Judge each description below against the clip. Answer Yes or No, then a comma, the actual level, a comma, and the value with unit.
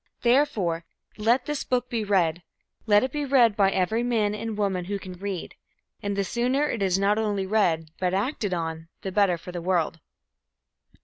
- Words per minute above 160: Yes, average, 185 wpm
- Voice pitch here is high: Yes, high, 200 Hz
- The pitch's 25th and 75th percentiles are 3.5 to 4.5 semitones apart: Yes, average, 4.1 semitones